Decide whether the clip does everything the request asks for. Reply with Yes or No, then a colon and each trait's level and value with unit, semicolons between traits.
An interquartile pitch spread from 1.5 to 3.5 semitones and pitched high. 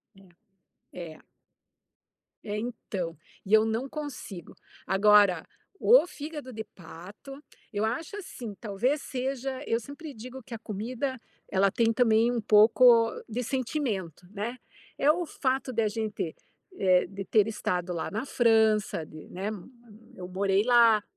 No: average, 4.3 semitones; high, 220 Hz